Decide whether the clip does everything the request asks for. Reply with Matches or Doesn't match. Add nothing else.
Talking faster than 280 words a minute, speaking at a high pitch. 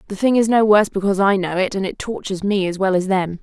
Matches